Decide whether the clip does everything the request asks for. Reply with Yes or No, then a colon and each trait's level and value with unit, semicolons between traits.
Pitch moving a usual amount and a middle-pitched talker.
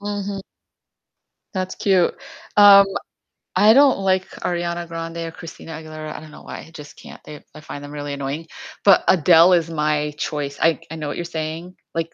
Yes: average, 3.3 semitones; medium, 165 Hz